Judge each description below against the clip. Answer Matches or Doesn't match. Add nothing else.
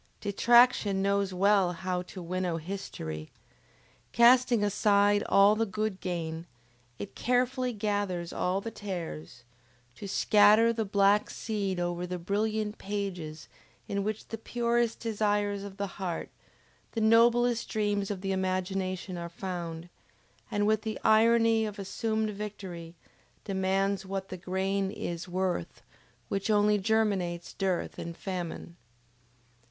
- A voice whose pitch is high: Matches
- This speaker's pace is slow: Matches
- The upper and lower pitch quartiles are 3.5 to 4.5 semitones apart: Doesn't match